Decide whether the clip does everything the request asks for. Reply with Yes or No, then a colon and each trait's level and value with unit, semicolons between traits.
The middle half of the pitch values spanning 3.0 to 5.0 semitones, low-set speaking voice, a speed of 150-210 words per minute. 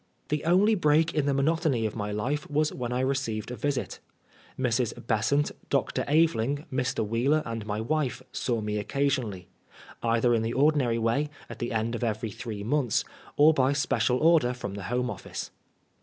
Yes: average, 4.3 semitones; low, 125 Hz; average, 175 wpm